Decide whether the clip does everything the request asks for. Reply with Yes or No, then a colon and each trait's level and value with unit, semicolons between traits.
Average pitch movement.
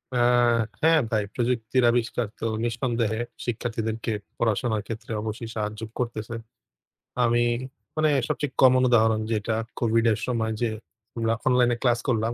No: narrow, 1.7 semitones